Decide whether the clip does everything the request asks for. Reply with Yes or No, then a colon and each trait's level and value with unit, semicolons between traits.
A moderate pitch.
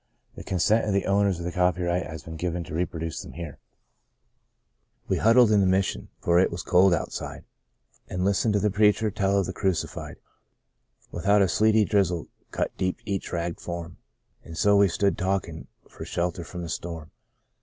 No: very low, 90 Hz